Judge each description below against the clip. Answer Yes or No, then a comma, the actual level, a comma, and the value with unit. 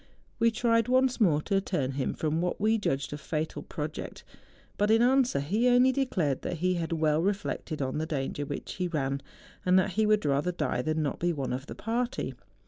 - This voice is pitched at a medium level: Yes, medium, 175 Hz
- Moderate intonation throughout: No, wide, 7.0 semitones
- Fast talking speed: Yes, fast, 215 wpm